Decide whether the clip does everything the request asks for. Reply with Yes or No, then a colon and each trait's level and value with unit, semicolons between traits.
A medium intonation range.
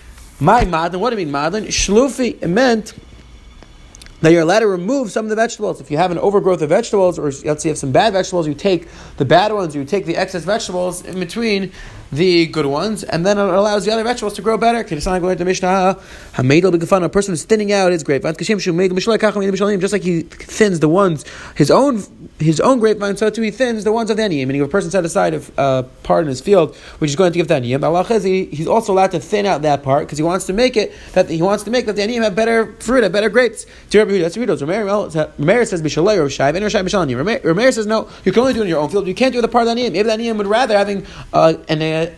Yes: average, 4.8 semitones